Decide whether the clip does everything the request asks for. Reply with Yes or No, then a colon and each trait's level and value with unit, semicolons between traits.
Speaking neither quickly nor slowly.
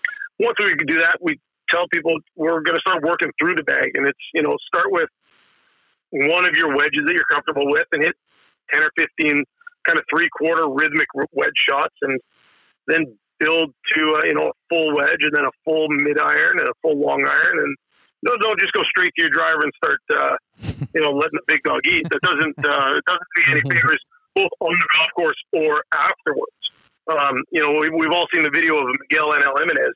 No: fast, 215 wpm